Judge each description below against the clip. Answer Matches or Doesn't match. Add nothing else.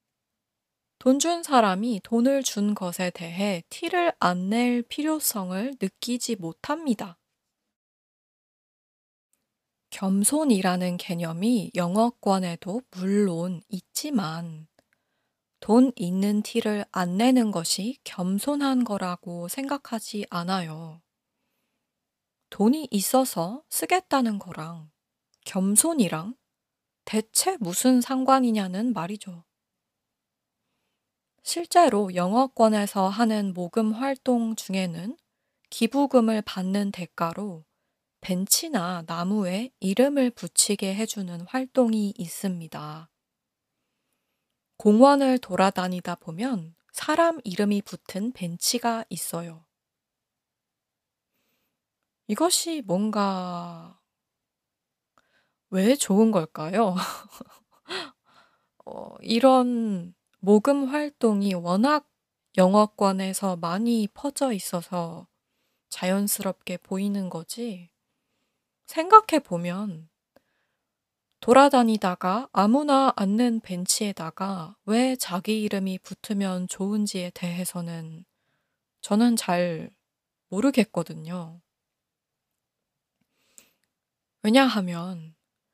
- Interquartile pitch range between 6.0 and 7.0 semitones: Doesn't match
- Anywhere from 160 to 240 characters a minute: Matches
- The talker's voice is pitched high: Matches